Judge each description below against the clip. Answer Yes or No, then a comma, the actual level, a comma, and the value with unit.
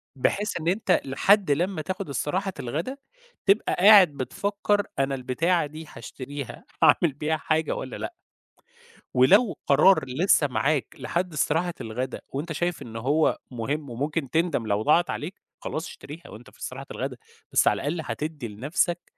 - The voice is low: No, medium, 155 Hz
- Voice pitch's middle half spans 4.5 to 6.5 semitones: Yes, average, 4.8 semitones